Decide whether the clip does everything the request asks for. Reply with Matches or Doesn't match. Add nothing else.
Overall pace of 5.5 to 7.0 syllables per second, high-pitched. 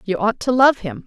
Doesn't match